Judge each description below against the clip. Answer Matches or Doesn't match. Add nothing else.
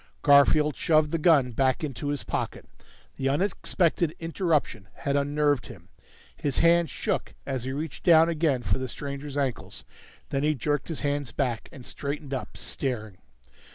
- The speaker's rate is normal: Matches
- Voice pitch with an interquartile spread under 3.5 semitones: Matches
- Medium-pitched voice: Matches